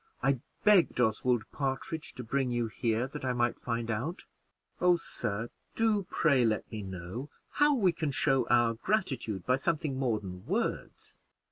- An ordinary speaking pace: Yes, average, 160 wpm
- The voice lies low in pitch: Yes, low, 125 Hz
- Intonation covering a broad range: Yes, wide, 5.9 semitones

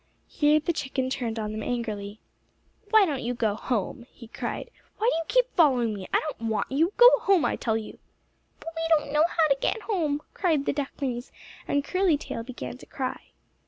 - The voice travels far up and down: Yes, wide, 5.8 semitones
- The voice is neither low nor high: No, very high, 275 Hz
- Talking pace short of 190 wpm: No, average, 200 wpm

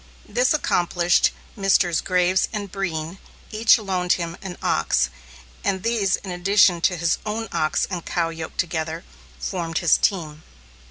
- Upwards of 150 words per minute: No, average, 145 wpm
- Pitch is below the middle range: No, medium, 180 Hz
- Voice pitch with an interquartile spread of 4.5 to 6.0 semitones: No, average, 2.8 semitones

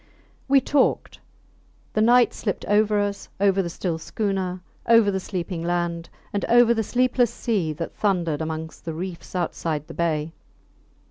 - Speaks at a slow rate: No, average, 150 wpm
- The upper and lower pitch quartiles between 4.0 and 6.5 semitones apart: Yes, average, 4.3 semitones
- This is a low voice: No, high, 190 Hz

